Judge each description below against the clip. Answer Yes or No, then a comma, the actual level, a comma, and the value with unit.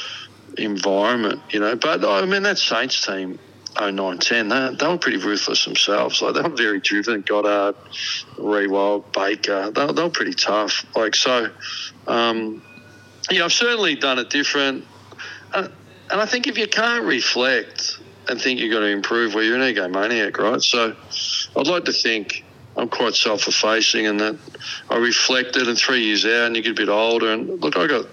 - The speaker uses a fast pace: No, average, 185 wpm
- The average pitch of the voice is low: Yes, low, 115 Hz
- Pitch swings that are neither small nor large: Yes, average, 4.1 semitones